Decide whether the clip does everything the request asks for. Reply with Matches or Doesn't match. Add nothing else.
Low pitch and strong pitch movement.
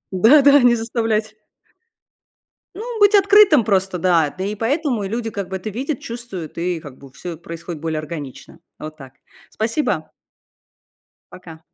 Doesn't match